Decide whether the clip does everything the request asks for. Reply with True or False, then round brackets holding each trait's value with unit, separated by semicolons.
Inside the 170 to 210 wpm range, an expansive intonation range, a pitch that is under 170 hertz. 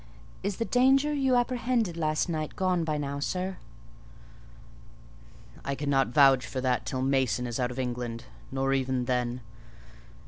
False (145 wpm; 6.5 semitones; 140 Hz)